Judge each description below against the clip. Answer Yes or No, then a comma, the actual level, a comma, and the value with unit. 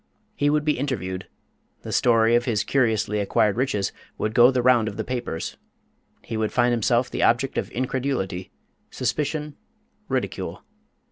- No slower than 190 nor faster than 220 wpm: No, average, 150 wpm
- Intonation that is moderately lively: Yes, average, 3.6 semitones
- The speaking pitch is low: Yes, low, 120 Hz